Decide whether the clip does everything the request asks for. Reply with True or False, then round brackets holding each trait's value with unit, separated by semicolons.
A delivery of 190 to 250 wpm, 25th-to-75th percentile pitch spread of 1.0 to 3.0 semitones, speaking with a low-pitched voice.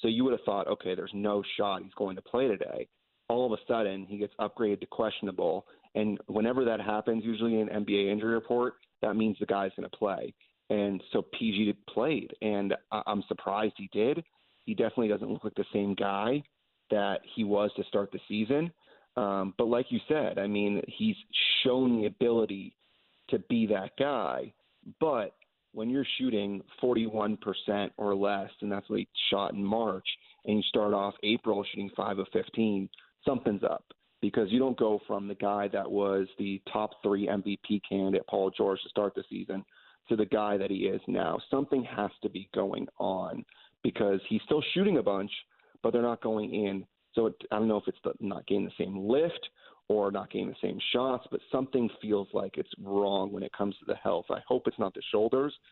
True (200 wpm; 2.7 semitones; 105 Hz)